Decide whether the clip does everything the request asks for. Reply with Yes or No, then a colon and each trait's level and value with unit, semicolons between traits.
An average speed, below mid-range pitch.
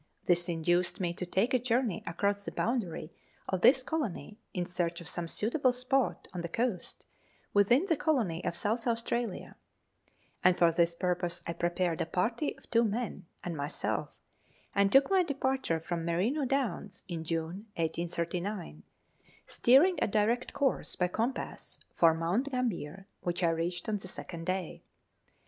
No: average, 160 wpm; high, 190 Hz